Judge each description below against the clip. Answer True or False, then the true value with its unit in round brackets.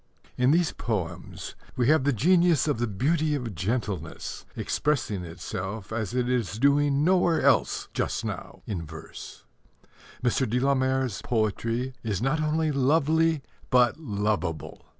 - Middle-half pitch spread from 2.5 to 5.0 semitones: False (5.6 semitones)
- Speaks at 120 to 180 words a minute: True (140 wpm)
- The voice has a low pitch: True (125 Hz)